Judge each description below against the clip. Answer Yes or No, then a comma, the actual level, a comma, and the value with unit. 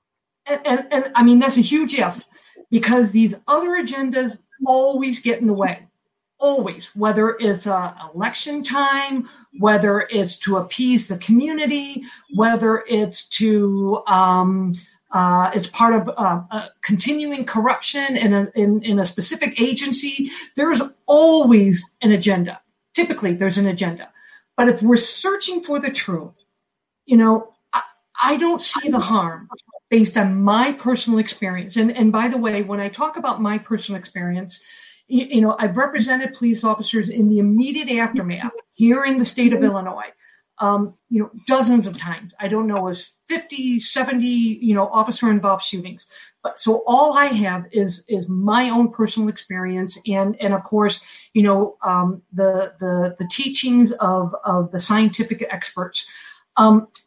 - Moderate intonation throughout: Yes, average, 4.4 semitones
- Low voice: No, high, 225 Hz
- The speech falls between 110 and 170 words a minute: Yes, average, 160 wpm